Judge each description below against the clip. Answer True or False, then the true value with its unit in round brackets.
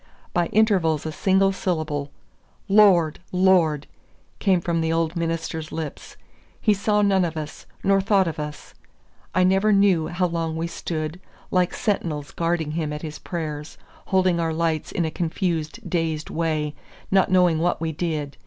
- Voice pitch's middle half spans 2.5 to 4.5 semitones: True (2.9 semitones)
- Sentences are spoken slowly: False (160 wpm)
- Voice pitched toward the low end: False (170 Hz)